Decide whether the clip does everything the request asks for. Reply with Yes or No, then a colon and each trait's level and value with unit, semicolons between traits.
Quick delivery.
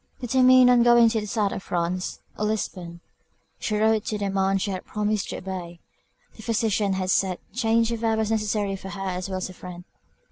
Yes: fast, 210 wpm